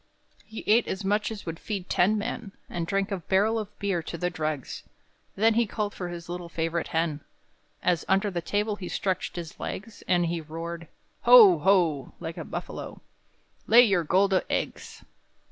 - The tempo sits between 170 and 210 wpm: Yes, average, 180 wpm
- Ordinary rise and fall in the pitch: Yes, average, 3.6 semitones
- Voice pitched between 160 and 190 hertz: Yes, medium, 185 Hz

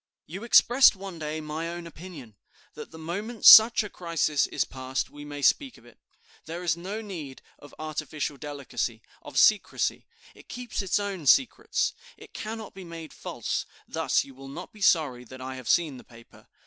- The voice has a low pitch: No, medium, 160 Hz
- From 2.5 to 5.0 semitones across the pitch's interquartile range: No, wide, 5.5 semitones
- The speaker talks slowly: No, average, 185 wpm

